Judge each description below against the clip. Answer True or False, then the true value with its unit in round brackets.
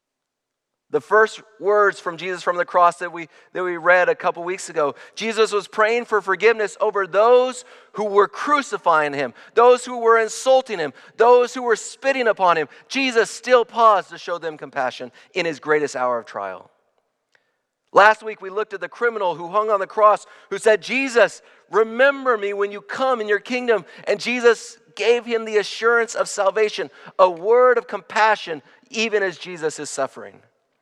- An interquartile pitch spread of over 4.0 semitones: True (4.6 semitones)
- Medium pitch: False (210 Hz)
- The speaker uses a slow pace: False (180 wpm)